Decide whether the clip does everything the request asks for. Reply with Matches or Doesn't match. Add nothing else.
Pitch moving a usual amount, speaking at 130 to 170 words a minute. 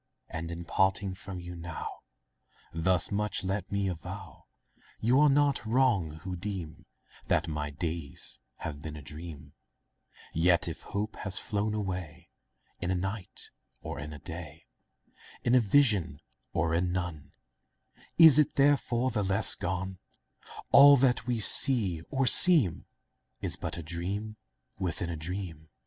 Matches